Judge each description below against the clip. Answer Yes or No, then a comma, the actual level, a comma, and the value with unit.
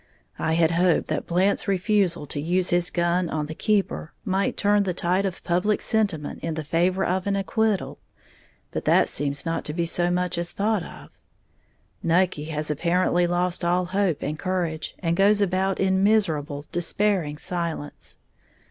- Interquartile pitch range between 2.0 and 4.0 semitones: Yes, average, 2.7 semitones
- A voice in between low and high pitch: Yes, medium, 175 Hz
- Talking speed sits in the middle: Yes, average, 165 wpm